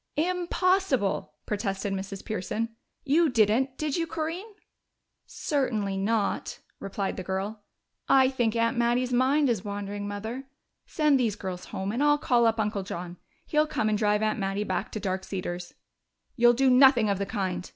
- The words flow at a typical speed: Yes, average, 160 wpm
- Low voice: No, high, 220 Hz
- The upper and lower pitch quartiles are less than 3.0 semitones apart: No, average, 5.2 semitones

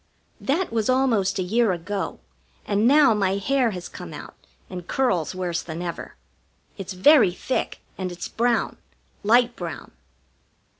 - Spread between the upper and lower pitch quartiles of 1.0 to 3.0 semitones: No, average, 5.1 semitones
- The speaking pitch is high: Yes, high, 205 Hz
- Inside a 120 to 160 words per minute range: Yes, average, 145 wpm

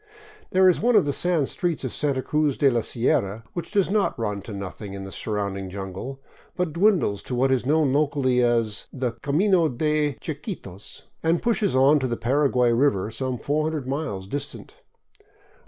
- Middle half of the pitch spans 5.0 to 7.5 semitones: Yes, average, 5.3 semitones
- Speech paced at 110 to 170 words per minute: No, average, 185 wpm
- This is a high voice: No, low, 135 Hz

